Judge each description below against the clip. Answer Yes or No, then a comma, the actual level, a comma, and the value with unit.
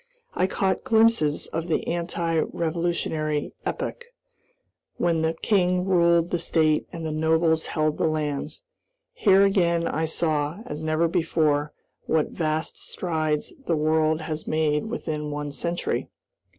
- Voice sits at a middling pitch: Yes, medium, 160 Hz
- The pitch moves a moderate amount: No, narrow, 1.9 semitones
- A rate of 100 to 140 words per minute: Yes, slow, 135 wpm